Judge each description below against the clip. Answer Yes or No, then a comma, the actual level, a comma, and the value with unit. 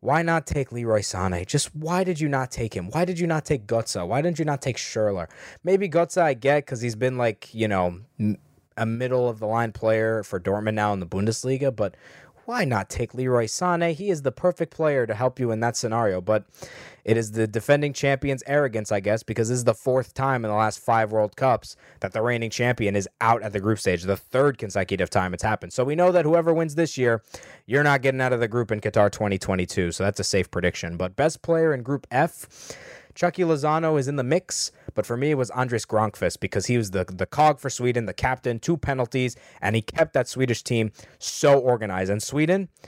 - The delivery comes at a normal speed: No, fast, 230 wpm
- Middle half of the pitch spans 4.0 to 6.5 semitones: Yes, average, 4.9 semitones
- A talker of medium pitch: No, low, 120 Hz